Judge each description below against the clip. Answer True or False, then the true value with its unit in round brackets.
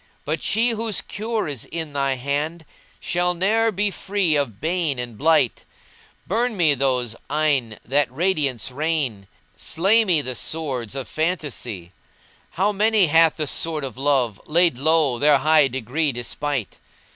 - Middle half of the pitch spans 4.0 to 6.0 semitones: True (5.1 semitones)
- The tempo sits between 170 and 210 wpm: False (155 wpm)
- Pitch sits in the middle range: True (150 Hz)